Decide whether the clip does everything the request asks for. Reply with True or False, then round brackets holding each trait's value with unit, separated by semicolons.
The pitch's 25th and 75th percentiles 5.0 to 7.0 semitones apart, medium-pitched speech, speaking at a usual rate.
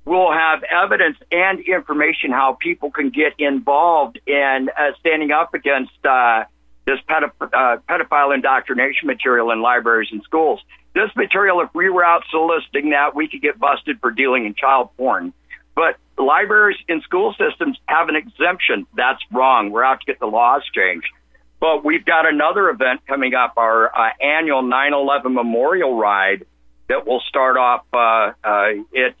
True (5.4 semitones; 145 Hz; 165 wpm)